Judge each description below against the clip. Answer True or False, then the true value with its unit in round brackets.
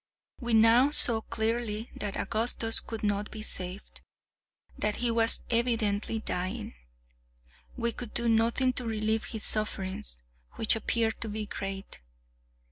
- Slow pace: True (130 wpm)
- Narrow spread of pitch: True (1.9 semitones)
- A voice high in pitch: True (220 Hz)